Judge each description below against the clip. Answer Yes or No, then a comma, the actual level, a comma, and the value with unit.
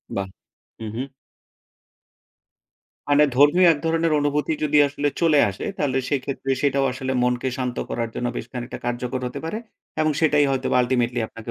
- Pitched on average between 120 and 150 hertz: Yes, low, 135 Hz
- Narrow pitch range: No, average, 3.1 semitones